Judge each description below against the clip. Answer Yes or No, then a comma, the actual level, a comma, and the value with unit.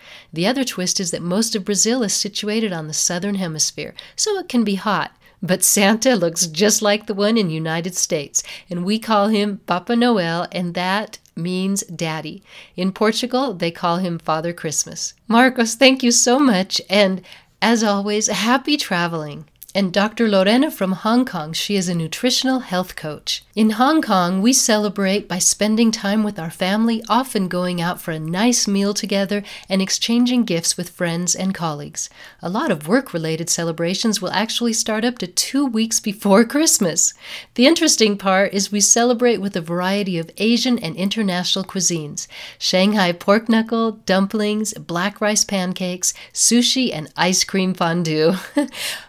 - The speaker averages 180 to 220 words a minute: No, average, 165 wpm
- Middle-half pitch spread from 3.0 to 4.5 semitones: Yes, average, 4.0 semitones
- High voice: Yes, high, 200 Hz